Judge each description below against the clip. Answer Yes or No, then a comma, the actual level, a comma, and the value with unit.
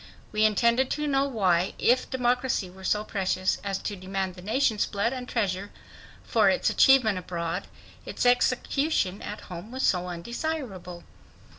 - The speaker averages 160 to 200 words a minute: No, average, 150 wpm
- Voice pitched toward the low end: No, high, 210 Hz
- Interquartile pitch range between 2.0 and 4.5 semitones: No, average, 5.2 semitones